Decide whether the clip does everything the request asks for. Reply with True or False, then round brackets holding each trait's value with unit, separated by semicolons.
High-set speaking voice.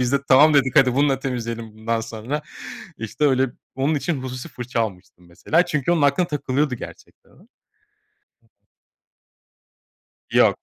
False (130 Hz)